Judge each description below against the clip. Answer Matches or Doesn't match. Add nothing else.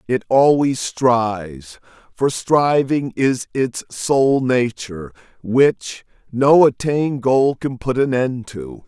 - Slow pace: Matches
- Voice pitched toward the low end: Matches